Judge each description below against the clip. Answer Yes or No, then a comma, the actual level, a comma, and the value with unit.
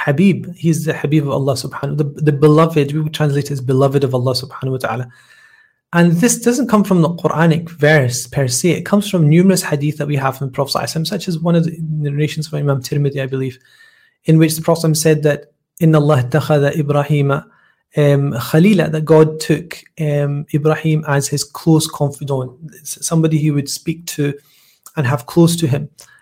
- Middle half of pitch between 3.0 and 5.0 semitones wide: No, narrow, 2.5 semitones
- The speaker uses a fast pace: No, average, 185 wpm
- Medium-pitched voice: Yes, medium, 150 Hz